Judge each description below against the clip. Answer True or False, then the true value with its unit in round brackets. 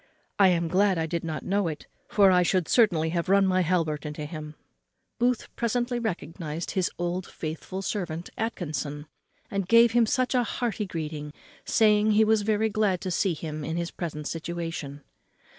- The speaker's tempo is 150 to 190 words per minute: True (170 wpm)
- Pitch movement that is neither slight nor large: True (4.7 semitones)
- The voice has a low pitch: False (180 Hz)